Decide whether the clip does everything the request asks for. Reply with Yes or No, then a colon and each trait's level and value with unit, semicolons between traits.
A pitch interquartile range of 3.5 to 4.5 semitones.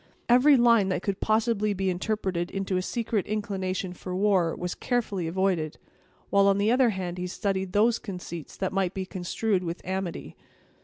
No: average, 2.8 semitones